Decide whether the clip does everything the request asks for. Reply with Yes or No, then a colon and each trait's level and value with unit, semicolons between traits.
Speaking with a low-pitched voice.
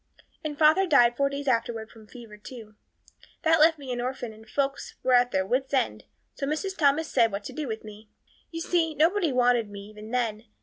No: very high, 250 Hz